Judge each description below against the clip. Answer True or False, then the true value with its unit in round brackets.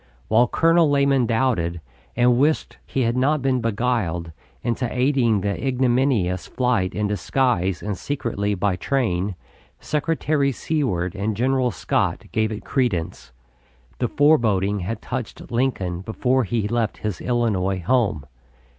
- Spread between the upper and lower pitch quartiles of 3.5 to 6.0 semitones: True (4.8 semitones)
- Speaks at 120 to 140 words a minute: True (135 wpm)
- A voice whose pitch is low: True (115 Hz)